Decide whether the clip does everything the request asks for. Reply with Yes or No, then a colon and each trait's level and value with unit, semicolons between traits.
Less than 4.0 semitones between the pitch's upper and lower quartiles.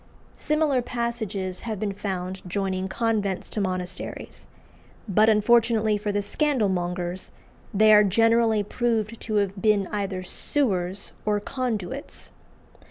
Yes: average, 3.2 semitones